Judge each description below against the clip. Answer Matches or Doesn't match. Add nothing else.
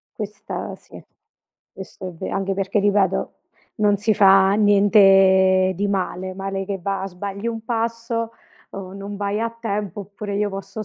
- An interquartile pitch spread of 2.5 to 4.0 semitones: Doesn't match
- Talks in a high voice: Matches